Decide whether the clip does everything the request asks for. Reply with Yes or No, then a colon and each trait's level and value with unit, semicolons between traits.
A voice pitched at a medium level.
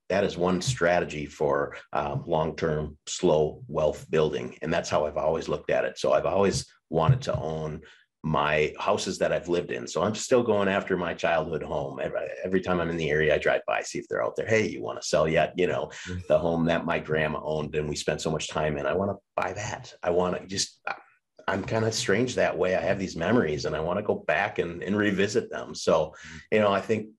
No: very low, 90 Hz